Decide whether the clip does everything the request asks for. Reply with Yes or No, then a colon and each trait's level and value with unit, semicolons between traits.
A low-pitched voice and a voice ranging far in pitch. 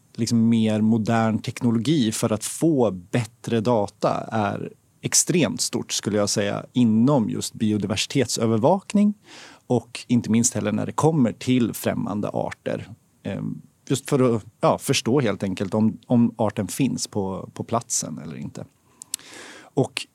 No: low, 115 Hz; narrow, 2.5 semitones